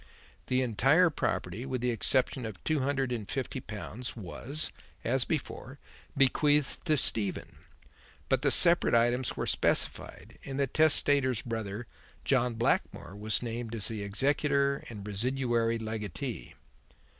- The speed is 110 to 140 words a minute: Yes, slow, 135 wpm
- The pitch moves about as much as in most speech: Yes, average, 3.6 semitones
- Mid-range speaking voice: No, low, 125 Hz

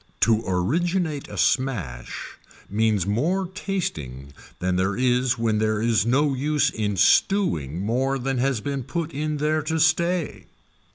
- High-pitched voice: No, low, 130 Hz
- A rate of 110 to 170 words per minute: Yes, average, 145 wpm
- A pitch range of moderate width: No, wide, 6.8 semitones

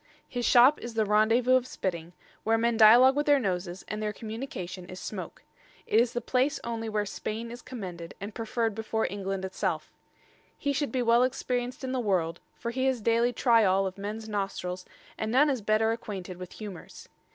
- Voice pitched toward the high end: Yes, high, 225 Hz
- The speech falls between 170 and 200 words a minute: Yes, average, 190 wpm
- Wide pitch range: No, average, 3.8 semitones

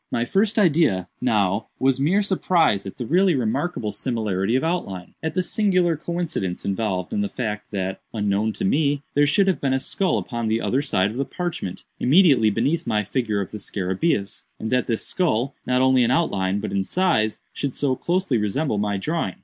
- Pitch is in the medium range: No, low, 125 Hz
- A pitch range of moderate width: No, wide, 8.0 semitones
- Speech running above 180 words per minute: Yes, average, 190 wpm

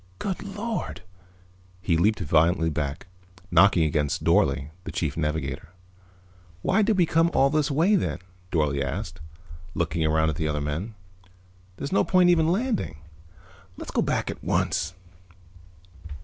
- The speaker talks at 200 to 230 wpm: No, average, 145 wpm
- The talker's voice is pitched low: Yes, very low, 85 Hz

